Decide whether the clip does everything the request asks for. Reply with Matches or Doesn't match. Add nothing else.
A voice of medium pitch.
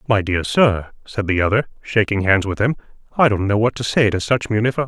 Doesn't match